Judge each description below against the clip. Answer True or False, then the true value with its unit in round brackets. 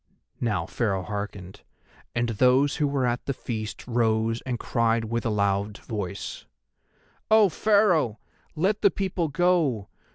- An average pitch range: False (6.1 semitones)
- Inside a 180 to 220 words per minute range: False (135 wpm)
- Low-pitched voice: True (120 Hz)